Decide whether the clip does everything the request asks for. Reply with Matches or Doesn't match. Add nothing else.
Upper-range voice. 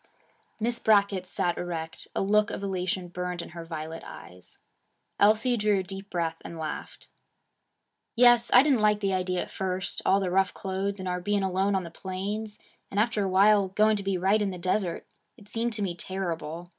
Matches